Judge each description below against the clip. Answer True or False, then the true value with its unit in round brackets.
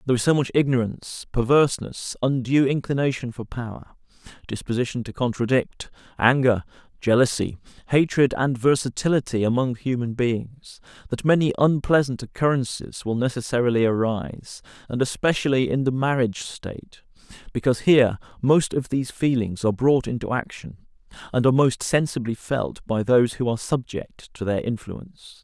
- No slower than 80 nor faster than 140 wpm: True (135 wpm)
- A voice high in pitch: False (125 Hz)